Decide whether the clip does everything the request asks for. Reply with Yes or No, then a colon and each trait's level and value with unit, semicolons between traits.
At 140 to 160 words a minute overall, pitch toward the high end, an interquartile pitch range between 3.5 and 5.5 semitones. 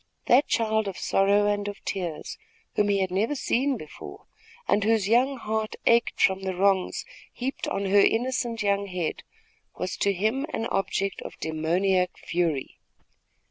No: average, 155 wpm; high, 200 Hz; average, 3.1 semitones